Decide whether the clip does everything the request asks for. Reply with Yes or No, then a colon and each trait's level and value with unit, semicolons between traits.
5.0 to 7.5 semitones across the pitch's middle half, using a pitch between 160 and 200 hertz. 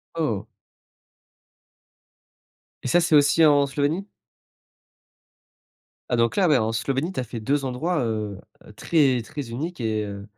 No: wide, 5.4 semitones; low, 135 Hz